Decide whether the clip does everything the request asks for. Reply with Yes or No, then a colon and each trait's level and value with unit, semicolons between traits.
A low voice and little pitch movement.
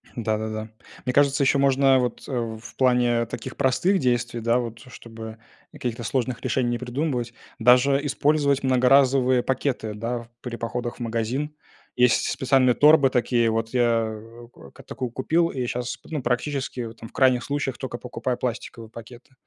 Yes: low, 125 Hz; narrow, 2.3 semitones